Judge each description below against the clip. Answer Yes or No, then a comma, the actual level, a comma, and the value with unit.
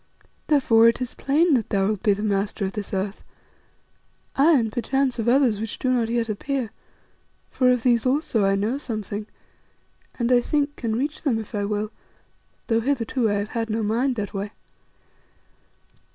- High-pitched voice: Yes, high, 230 Hz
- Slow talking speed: No, average, 180 wpm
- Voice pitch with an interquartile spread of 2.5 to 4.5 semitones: Yes, average, 3.6 semitones